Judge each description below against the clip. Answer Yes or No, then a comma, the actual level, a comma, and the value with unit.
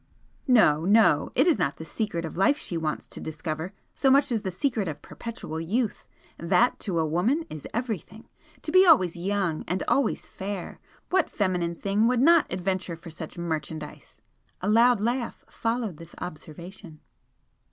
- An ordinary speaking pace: Yes, average, 165 wpm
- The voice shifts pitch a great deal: Yes, wide, 6.1 semitones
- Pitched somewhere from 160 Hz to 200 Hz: Yes, high, 190 Hz